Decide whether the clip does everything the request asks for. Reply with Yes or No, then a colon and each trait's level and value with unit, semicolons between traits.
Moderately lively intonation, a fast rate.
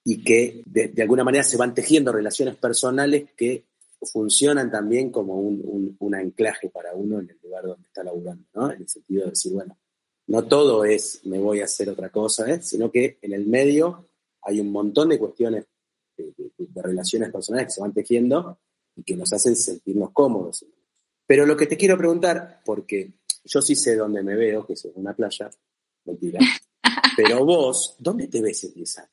No: wide, 6.6 semitones; fast, 200 wpm